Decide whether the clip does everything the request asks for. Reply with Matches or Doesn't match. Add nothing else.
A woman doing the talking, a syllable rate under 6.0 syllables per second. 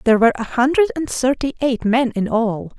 Matches